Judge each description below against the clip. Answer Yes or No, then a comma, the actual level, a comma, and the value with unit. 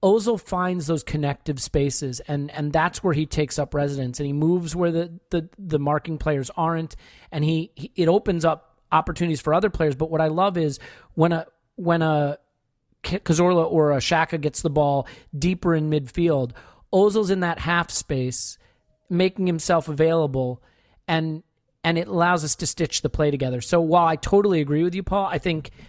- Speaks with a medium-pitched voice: Yes, medium, 160 Hz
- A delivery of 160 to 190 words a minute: Yes, average, 185 wpm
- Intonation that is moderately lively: Yes, average, 3.0 semitones